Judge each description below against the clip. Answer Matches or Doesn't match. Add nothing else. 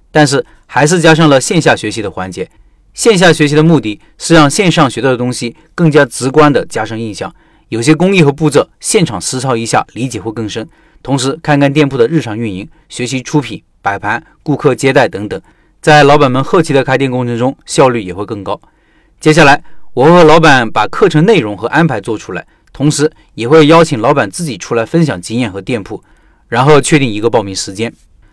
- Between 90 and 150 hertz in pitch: Matches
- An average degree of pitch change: Matches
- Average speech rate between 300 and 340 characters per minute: Matches